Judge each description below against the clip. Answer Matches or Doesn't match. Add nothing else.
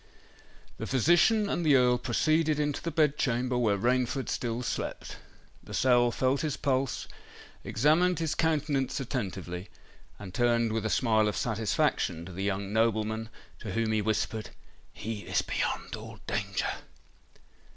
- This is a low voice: Matches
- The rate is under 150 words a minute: Matches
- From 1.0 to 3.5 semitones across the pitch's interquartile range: Doesn't match